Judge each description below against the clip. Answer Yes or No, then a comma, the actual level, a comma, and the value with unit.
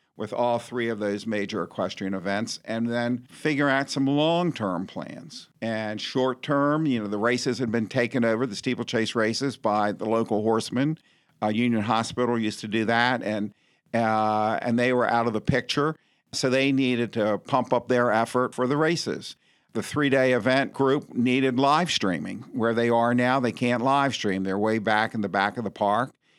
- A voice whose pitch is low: Yes, low, 120 Hz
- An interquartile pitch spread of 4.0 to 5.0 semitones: No, average, 3.2 semitones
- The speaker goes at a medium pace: Yes, average, 195 wpm